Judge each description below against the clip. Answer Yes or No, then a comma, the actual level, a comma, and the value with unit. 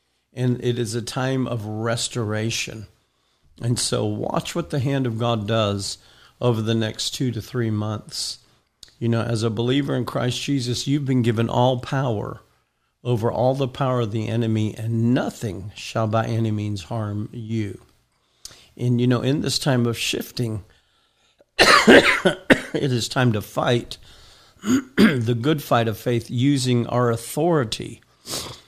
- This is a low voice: Yes, low, 120 Hz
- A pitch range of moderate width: No, narrow, 2.3 semitones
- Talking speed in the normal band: Yes, average, 150 wpm